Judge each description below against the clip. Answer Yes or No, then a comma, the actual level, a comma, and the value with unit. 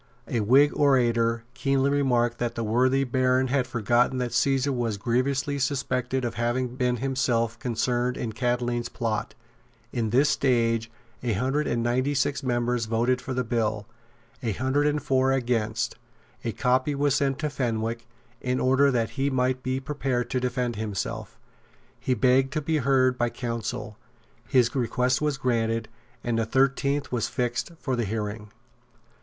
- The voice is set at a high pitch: No, low, 125 Hz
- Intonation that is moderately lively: No, narrow, 2.2 semitones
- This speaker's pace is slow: No, average, 160 wpm